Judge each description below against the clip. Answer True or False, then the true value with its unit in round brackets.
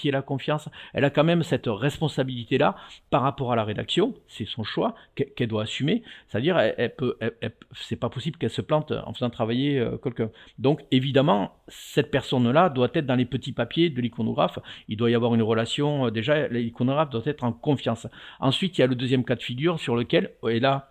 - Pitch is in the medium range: False (130 Hz)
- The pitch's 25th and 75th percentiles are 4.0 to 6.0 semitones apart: False (3.4 semitones)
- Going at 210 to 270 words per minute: True (220 wpm)